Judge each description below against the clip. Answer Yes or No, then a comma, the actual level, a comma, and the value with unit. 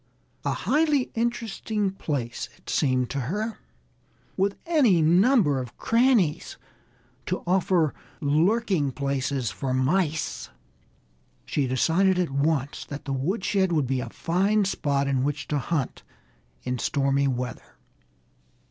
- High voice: No, medium, 155 Hz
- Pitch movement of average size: No, wide, 6.1 semitones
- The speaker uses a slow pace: Yes, slow, 120 wpm